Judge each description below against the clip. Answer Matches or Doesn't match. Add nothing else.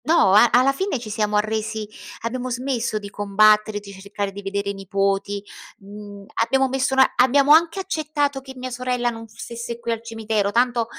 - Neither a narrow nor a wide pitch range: Matches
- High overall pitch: Matches